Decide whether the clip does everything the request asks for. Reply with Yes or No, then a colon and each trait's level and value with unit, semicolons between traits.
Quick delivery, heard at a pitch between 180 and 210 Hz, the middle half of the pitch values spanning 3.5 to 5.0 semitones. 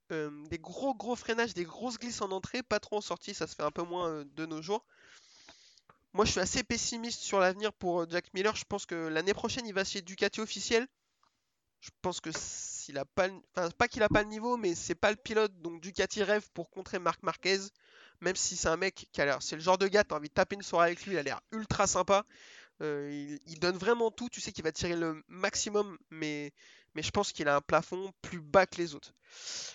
Yes: fast, 245 wpm; high, 190 Hz; average, 4.2 semitones